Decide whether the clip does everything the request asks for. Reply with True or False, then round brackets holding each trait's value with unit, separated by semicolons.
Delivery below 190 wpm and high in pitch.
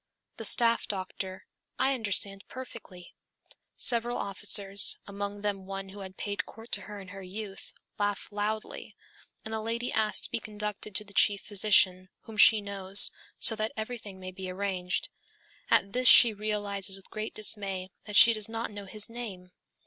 True (170 wpm; 205 Hz)